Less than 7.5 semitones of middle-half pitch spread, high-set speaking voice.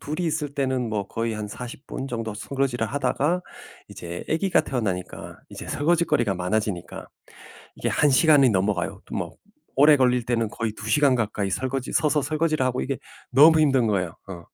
No: average, 5.2 semitones; low, 125 Hz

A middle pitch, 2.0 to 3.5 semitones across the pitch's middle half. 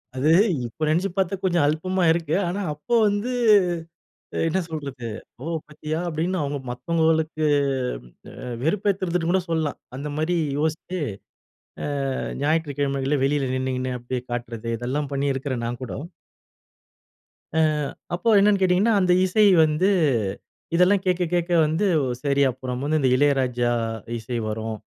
No: medium, 155 Hz; average, 5.0 semitones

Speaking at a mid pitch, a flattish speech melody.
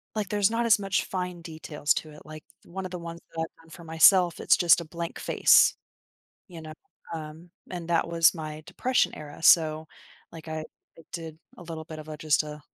Yes: medium, 165 Hz; narrow, 2.1 semitones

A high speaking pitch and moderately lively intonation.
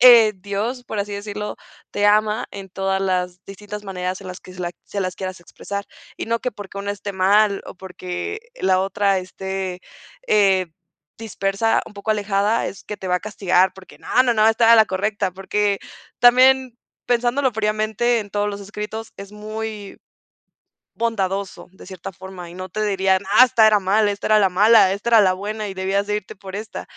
No: high, 200 Hz; narrow, 2.1 semitones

